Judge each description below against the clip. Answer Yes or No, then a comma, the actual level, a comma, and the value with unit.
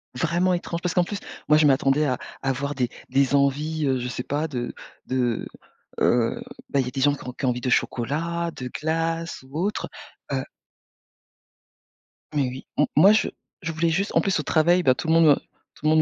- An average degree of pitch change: Yes, average, 4.0 semitones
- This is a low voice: No, medium, 150 Hz